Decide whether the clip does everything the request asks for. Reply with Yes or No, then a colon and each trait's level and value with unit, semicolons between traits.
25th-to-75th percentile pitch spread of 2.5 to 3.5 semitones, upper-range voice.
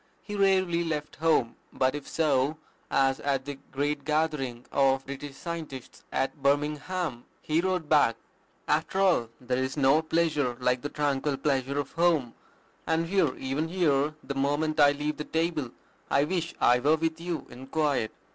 No: average, 3.1 semitones; medium, 145 Hz